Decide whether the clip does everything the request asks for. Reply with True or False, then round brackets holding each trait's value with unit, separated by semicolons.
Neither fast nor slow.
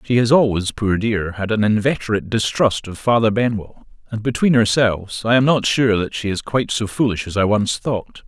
False (210 wpm)